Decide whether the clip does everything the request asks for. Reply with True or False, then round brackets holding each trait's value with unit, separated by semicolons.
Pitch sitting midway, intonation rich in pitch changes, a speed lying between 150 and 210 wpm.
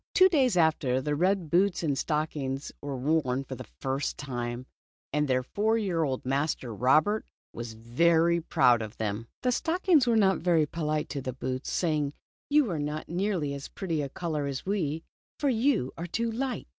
True (155 Hz; 6.3 semitones; 195 wpm)